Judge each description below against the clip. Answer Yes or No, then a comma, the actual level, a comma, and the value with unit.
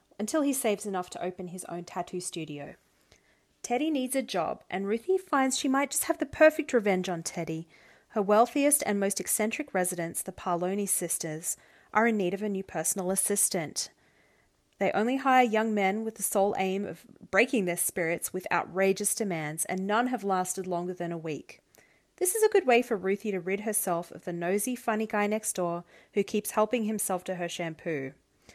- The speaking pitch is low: No, high, 195 Hz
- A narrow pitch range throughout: No, average, 4.2 semitones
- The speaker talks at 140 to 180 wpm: No, average, 190 wpm